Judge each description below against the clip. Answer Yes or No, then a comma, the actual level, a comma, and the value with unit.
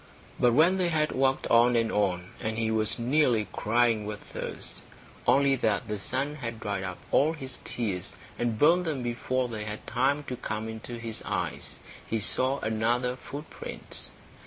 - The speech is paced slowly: No, average, 170 wpm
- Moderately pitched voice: No, low, 120 Hz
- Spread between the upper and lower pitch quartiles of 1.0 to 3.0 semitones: No, average, 3.6 semitones